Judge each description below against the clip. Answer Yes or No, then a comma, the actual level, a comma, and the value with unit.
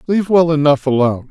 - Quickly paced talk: No, average, 185 wpm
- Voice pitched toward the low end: No, medium, 150 Hz